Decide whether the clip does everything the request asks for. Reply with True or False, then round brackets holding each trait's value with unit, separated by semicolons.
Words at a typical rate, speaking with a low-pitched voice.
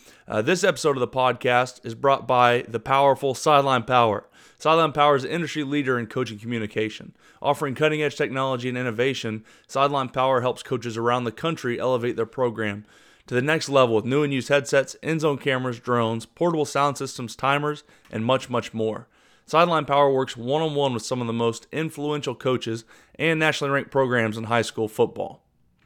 True (185 wpm; 130 Hz)